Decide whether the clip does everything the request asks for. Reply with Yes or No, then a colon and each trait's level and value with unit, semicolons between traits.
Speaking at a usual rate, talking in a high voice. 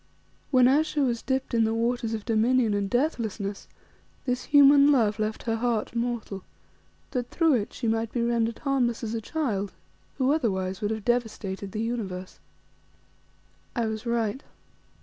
Yes: average, 155 wpm; high, 230 Hz